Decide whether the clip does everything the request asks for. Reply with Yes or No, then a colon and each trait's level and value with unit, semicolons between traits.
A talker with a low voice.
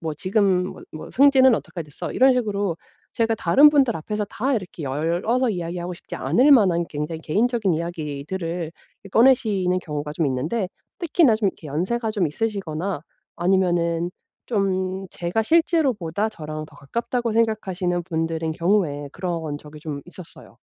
No: medium, 185 Hz